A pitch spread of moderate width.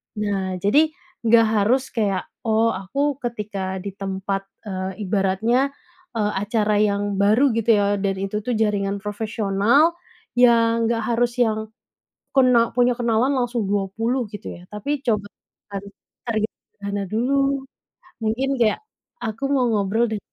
Yes: average, 3.2 semitones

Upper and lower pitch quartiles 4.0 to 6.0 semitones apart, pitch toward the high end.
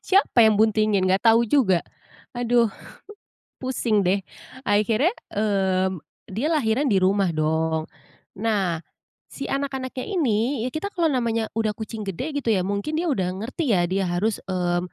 Yes: average, 5.2 semitones; high, 215 Hz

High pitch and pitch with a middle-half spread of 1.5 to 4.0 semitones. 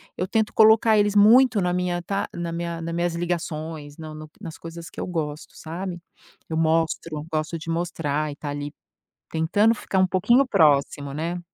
No: medium, 170 Hz; average, 2.9 semitones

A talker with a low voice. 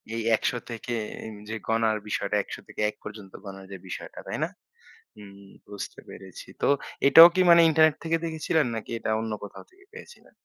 Yes: low, 110 Hz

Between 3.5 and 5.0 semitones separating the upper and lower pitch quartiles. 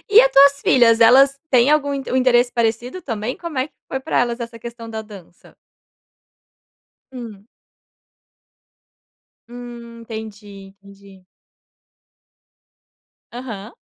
No: average, 2.9 semitones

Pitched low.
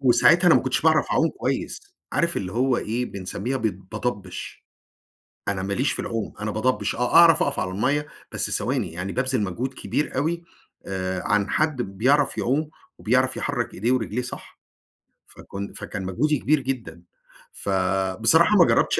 Yes: low, 120 Hz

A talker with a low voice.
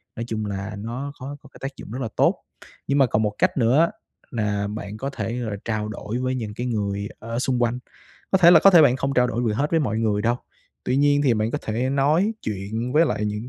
Yes: low, 120 Hz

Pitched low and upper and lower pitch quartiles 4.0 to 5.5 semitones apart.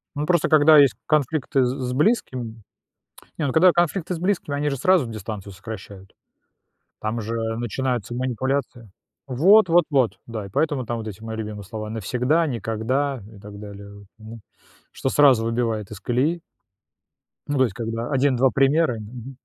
Yes: low, 125 Hz; average, 4.6 semitones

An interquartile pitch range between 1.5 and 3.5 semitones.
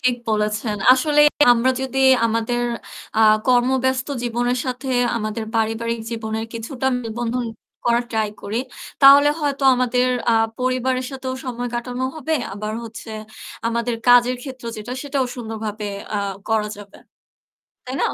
Yes: narrow, 2.5 semitones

